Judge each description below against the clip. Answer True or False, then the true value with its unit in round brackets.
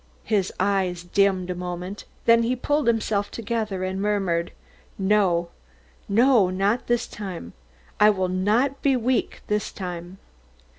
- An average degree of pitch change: True (3.7 semitones)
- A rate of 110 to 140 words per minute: True (135 wpm)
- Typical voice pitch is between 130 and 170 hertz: False (200 Hz)